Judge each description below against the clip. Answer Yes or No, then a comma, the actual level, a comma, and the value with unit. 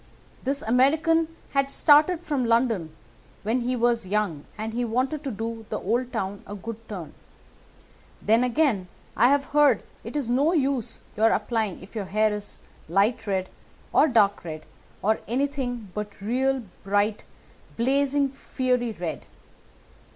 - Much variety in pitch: No, average, 4.4 semitones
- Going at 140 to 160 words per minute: Yes, average, 145 wpm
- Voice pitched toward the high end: Yes, high, 235 Hz